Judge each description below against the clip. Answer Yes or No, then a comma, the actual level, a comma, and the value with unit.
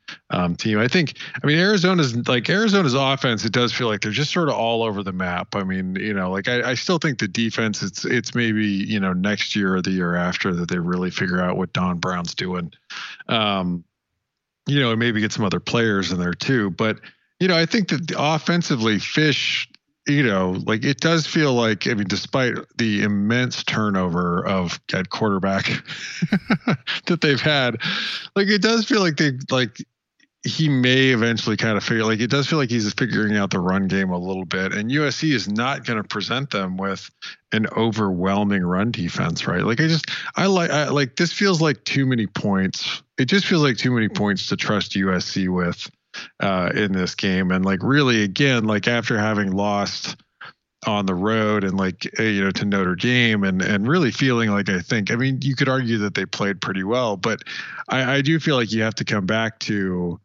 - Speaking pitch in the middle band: No, low, 110 Hz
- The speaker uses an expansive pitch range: Yes, wide, 6.2 semitones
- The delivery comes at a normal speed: No, fast, 210 wpm